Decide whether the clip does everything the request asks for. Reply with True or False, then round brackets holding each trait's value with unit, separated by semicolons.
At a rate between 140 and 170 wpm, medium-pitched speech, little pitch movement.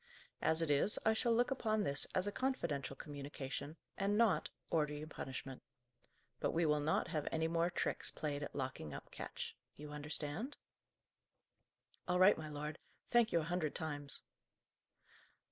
False (160 wpm; 155 Hz; 4.3 semitones)